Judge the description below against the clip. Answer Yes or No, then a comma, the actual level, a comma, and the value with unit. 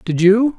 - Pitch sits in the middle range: No, high, 210 Hz